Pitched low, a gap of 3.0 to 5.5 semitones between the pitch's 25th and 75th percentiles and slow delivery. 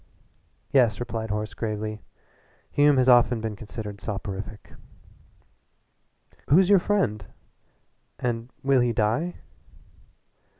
Yes: low, 115 Hz; average, 3.6 semitones; slow, 100 wpm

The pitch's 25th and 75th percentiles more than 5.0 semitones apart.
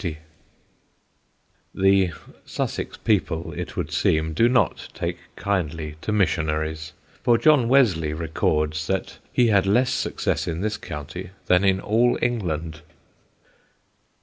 Yes: wide, 5.5 semitones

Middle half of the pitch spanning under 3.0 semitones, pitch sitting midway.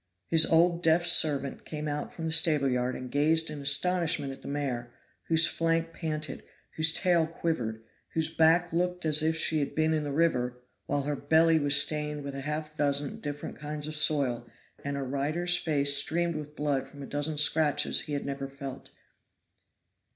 Yes: narrow, 2.4 semitones; medium, 150 Hz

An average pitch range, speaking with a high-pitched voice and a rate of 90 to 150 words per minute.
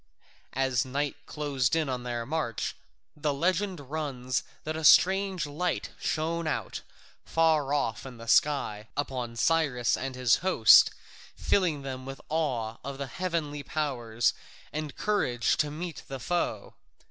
No: average, 4.0 semitones; medium, 145 Hz; average, 140 wpm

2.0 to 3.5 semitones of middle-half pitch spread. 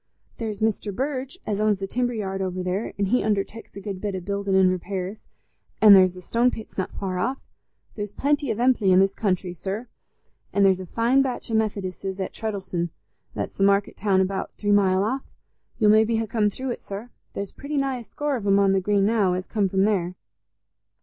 Yes: average, 2.9 semitones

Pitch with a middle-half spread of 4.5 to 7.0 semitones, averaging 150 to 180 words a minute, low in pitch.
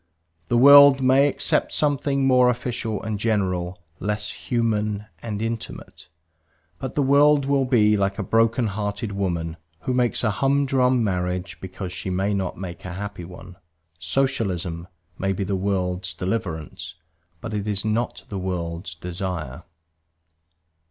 No: average, 4.9 semitones; average, 140 wpm; low, 105 Hz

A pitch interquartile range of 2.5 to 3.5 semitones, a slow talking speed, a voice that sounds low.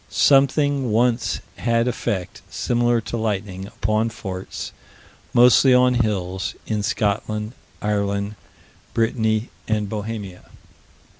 Yes: average, 2.9 semitones; slow, 95 wpm; low, 110 Hz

